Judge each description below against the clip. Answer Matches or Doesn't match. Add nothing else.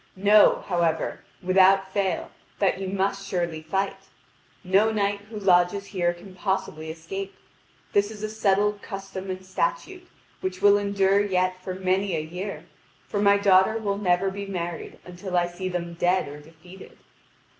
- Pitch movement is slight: Matches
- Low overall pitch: Doesn't match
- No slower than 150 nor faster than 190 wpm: Matches